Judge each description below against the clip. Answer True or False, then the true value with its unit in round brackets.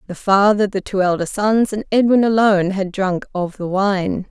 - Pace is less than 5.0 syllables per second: True (4.7 syllables/s)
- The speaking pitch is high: True (195 Hz)